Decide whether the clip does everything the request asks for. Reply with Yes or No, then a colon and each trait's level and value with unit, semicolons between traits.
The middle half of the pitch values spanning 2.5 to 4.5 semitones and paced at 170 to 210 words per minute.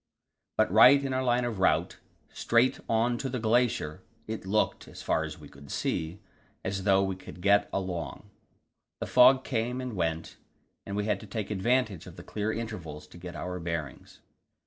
No: average, 5.0 semitones; average, 185 wpm